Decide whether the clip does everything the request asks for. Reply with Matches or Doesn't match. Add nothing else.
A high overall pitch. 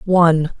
Doesn't match